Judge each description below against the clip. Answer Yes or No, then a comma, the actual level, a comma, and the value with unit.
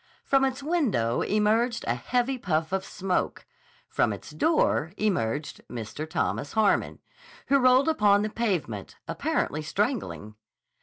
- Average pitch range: No, wide, 8.5 semitones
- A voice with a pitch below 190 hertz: No, high, 210 Hz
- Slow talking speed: Yes, slow, 130 wpm